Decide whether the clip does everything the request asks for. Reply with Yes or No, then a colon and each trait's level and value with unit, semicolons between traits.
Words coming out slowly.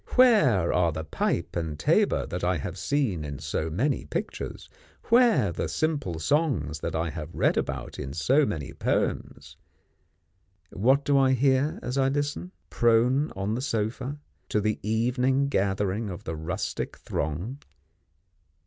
No: average, 150 wpm